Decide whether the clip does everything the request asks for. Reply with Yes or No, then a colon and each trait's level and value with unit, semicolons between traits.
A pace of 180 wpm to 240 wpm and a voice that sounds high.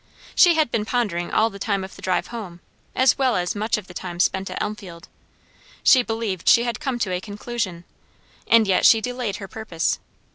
Yes: fast, 205 wpm; high, 210 Hz